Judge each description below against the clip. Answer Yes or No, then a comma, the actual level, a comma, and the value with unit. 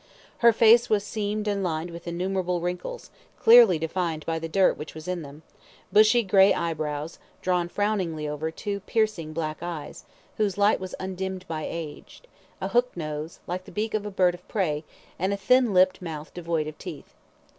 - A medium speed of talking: Yes, average, 180 wpm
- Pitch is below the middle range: No, medium, 180 Hz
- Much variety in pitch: No, average, 4.0 semitones